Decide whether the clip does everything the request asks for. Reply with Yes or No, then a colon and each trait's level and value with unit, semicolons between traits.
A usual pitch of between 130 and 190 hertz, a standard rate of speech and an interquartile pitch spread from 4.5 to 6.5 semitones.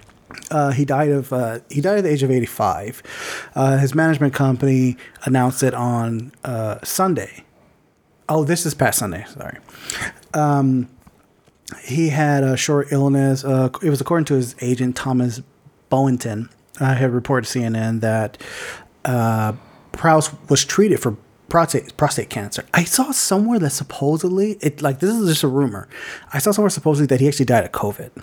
No: low, 135 Hz; average, 170 wpm; average, 3.5 semitones